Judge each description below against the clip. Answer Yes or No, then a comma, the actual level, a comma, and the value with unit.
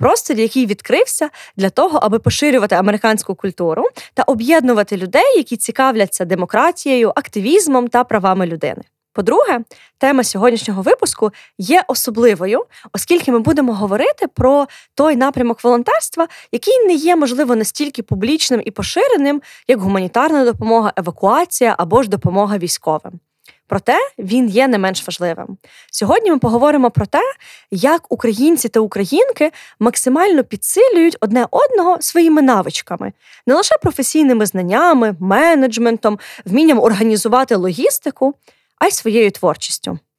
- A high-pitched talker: Yes, high, 245 Hz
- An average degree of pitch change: No, wide, 6.5 semitones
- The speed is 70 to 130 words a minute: Yes, average, 120 wpm